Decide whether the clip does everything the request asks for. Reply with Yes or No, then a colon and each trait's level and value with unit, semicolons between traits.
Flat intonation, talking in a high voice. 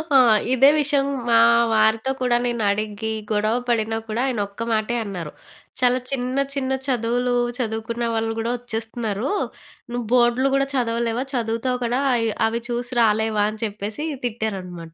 Yes: narrow, 2.1 semitones; high, 230 Hz